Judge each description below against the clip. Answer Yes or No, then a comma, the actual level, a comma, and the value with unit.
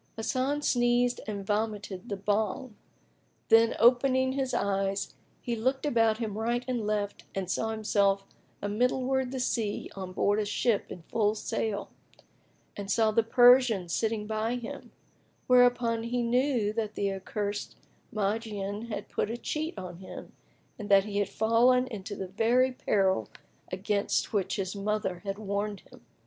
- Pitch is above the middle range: Yes, high, 215 Hz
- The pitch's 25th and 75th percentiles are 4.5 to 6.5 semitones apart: No, average, 3.2 semitones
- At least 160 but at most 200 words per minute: No, average, 150 wpm